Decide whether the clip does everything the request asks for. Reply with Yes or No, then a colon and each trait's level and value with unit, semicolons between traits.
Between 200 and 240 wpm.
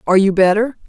Yes: fast, 205 wpm